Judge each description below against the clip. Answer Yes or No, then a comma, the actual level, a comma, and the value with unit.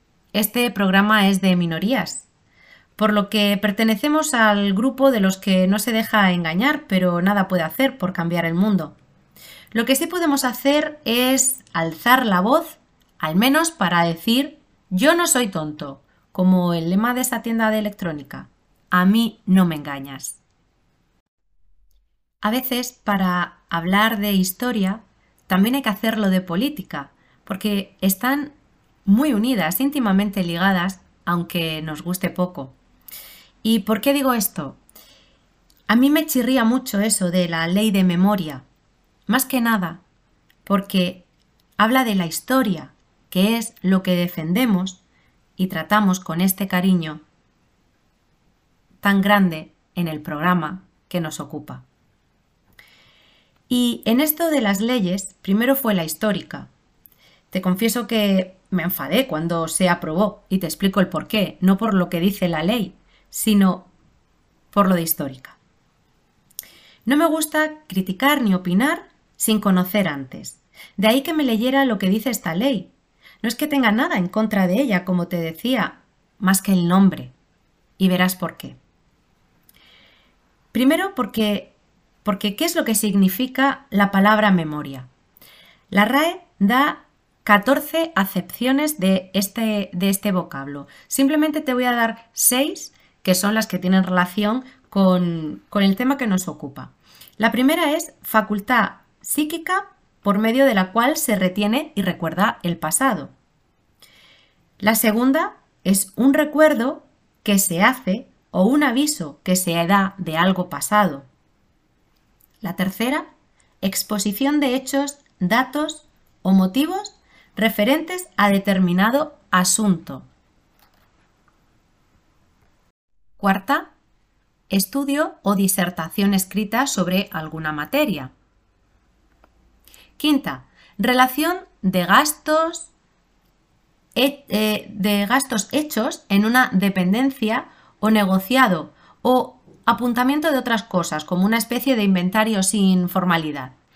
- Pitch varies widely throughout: Yes, wide, 5.7 semitones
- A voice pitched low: No, high, 205 Hz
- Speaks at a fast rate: No, average, 130 wpm